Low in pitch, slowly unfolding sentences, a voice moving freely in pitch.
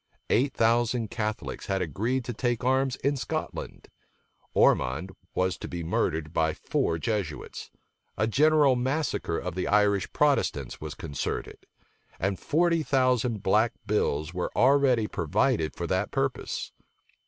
Yes: low, 110 Hz; slow, 130 wpm; wide, 6.3 semitones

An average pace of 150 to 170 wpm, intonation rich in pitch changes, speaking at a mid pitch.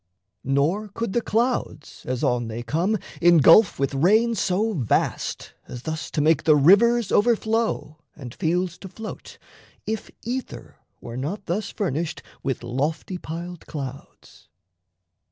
No: slow, 135 wpm; wide, 6.9 semitones; medium, 170 Hz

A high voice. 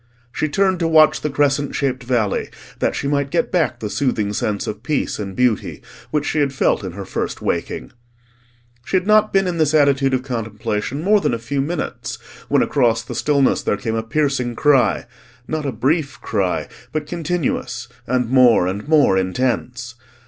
No: low, 135 Hz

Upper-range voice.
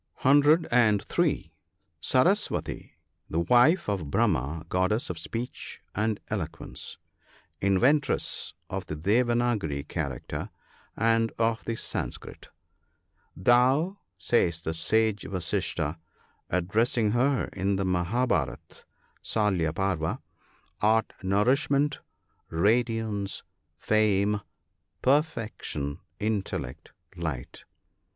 No: low, 105 Hz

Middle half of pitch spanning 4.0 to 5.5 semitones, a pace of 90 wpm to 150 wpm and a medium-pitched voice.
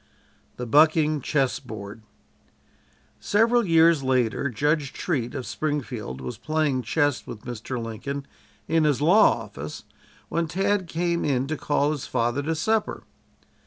Yes: average, 4.9 semitones; slow, 135 wpm; medium, 145 Hz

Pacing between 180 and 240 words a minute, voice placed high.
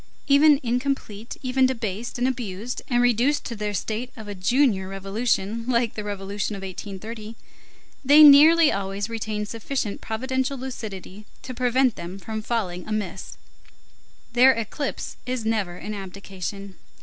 No: slow, 135 wpm; high, 220 Hz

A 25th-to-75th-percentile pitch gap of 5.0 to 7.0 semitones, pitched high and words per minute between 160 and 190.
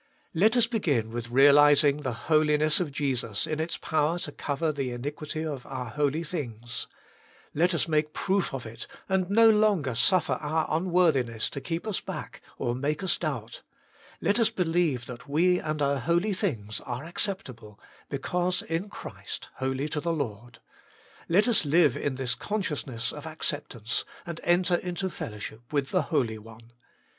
No: wide, 5.5 semitones; medium, 150 Hz; average, 165 wpm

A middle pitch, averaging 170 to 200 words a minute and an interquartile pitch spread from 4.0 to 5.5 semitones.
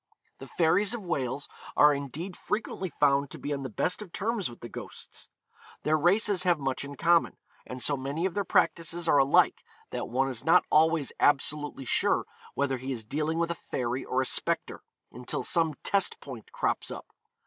Yes: medium, 150 Hz; average, 190 wpm; average, 4.4 semitones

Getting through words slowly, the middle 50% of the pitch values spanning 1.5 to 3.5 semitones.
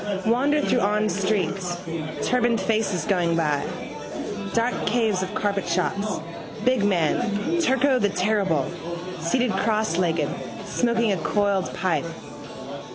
No: slow, 110 wpm; average, 4.1 semitones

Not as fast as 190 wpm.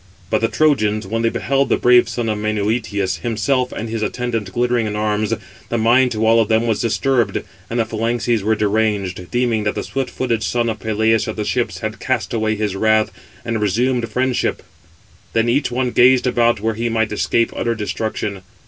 No: average, 195 wpm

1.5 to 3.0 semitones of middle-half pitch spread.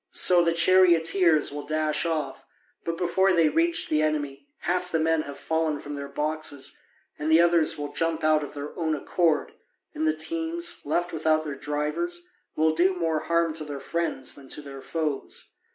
Yes: narrow, 2.4 semitones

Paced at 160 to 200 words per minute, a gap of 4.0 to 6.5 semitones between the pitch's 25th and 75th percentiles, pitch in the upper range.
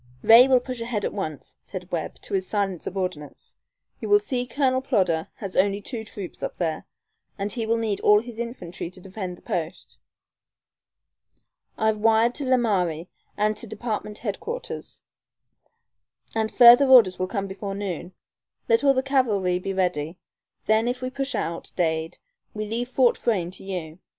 Yes: average, 165 wpm; average, 4.6 semitones; high, 210 Hz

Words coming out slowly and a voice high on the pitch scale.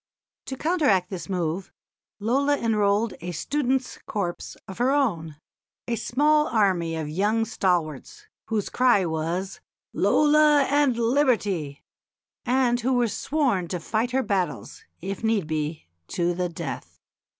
Yes: slow, 130 wpm; high, 210 Hz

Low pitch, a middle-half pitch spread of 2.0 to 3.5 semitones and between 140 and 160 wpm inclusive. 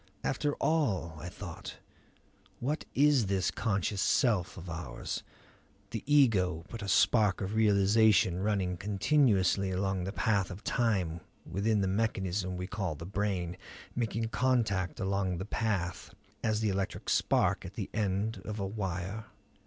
Yes: low, 100 Hz; average, 3.1 semitones; average, 145 wpm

